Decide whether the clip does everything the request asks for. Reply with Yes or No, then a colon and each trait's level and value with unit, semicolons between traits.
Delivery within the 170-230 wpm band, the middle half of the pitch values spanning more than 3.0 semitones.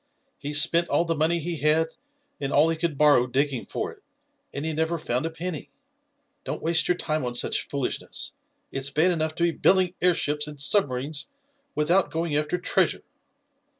No: average, 180 wpm; narrow, 2.6 semitones